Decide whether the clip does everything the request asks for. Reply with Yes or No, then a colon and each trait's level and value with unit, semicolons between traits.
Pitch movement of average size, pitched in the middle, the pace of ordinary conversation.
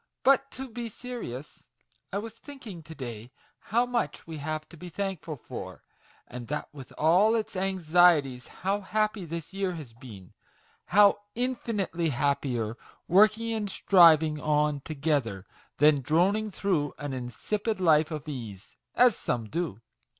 No: wide, 6.4 semitones; medium, 165 Hz; average, 145 wpm